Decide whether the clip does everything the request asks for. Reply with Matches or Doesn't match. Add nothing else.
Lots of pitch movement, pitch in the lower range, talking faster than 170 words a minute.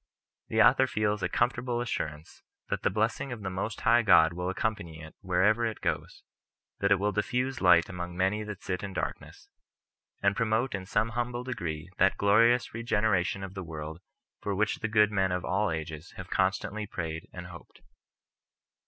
Doesn't match